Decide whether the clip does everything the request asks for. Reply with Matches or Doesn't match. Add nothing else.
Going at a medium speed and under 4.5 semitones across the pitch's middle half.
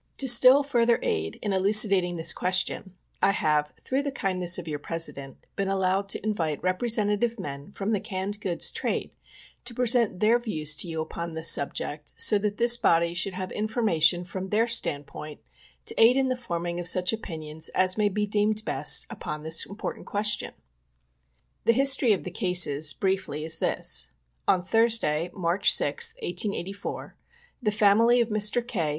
Doesn't match